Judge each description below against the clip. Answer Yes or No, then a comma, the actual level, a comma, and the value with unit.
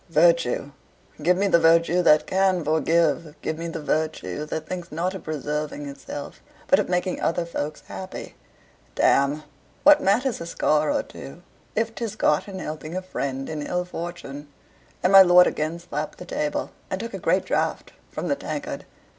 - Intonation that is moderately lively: Yes, average, 3.2 semitones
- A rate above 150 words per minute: Yes, average, 175 wpm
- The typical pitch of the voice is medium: Yes, medium, 165 Hz